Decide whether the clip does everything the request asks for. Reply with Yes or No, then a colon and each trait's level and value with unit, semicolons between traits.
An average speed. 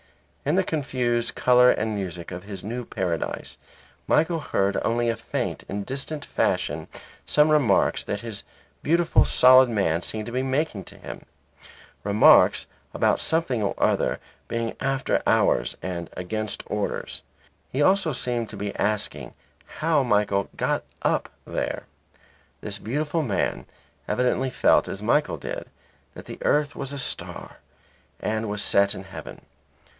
Yes: average, 145 wpm